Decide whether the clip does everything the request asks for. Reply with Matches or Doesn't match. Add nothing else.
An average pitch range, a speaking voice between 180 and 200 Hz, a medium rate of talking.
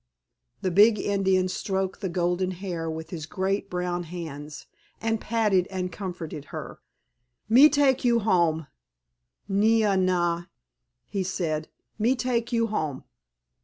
Doesn't match